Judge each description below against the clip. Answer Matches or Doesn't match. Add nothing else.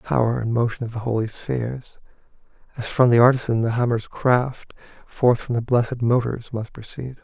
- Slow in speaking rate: Doesn't match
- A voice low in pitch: Matches